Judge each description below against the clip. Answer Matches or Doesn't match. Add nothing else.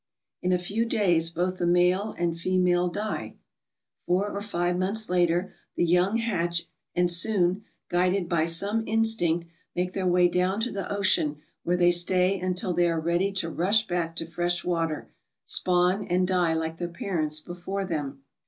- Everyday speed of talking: Matches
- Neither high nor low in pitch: Matches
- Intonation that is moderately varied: Doesn't match